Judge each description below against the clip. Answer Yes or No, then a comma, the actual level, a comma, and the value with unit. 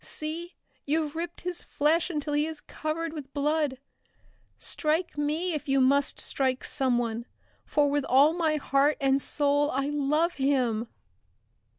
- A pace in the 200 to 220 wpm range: No, average, 145 wpm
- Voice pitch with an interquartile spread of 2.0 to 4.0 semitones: Yes, narrow, 2.4 semitones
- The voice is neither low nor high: No, very high, 295 Hz